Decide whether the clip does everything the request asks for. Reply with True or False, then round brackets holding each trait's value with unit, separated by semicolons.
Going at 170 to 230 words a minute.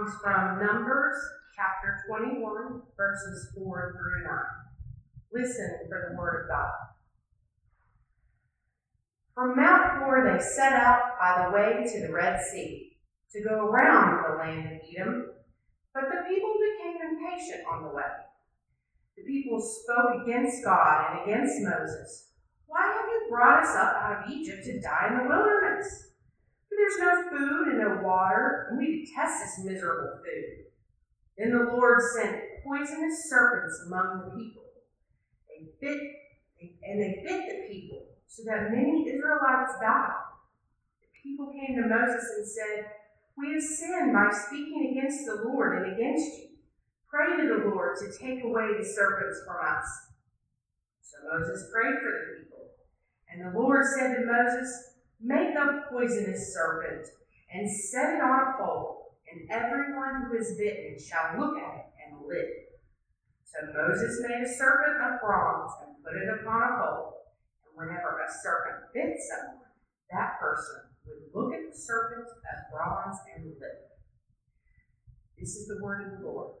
False (155 wpm)